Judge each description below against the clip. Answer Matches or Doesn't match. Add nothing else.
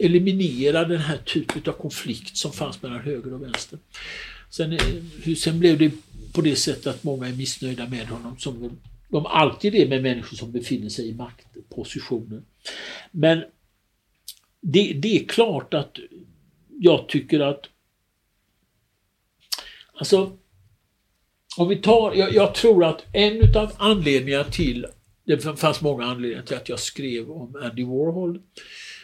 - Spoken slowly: Doesn't match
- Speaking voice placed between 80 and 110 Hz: Doesn't match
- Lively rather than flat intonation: Matches